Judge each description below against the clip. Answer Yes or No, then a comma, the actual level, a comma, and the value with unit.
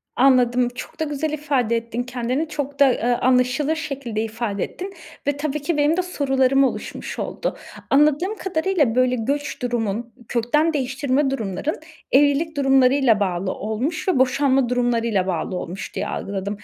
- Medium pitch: No, very high, 260 Hz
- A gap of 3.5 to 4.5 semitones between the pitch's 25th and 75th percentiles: Yes, average, 3.8 semitones